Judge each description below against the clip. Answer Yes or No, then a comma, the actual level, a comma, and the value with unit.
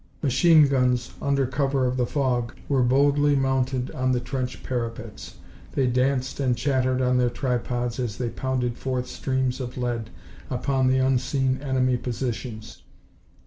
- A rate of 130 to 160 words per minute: Yes, average, 145 wpm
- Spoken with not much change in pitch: Yes, narrow, 1.4 semitones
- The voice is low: Yes, low, 130 Hz